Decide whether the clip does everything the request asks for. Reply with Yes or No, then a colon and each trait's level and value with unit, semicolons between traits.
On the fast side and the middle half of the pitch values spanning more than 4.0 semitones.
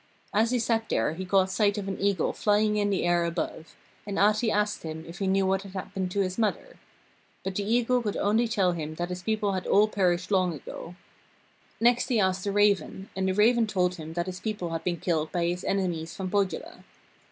No: fast, 220 wpm; average, 2.7 semitones